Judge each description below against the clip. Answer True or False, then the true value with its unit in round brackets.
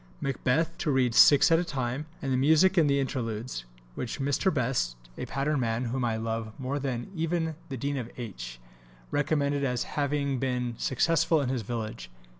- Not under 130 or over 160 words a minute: False (185 wpm)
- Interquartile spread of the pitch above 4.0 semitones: False (3.6 semitones)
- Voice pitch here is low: True (130 Hz)